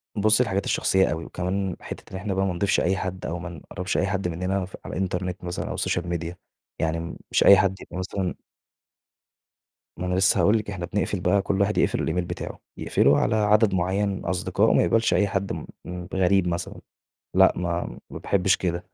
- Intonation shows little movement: Yes, narrow, 1.9 semitones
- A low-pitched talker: Yes, very low, 95 Hz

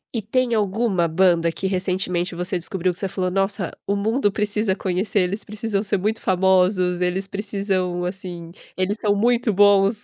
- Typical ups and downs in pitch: No, narrow, 2.2 semitones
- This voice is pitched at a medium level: No, high, 195 Hz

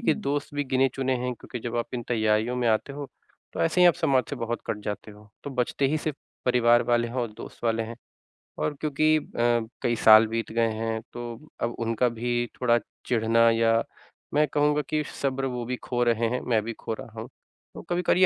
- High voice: No, low, 120 Hz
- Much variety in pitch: No, average, 2.9 semitones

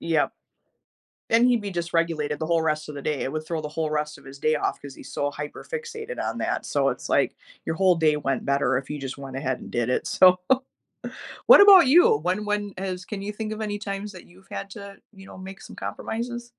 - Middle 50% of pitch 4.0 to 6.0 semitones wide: Yes, wide, 5.6 semitones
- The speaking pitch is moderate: Yes, medium, 175 Hz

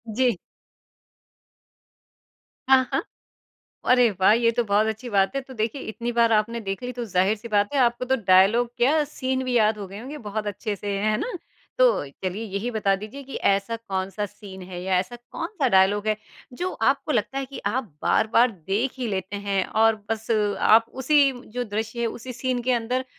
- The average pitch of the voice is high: Yes, high, 225 Hz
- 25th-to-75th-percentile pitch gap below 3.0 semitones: No, average, 3.7 semitones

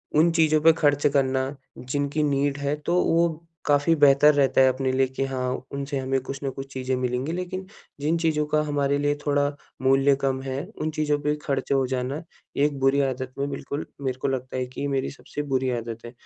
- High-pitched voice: No, medium, 140 Hz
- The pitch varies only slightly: Yes, narrow, 1.9 semitones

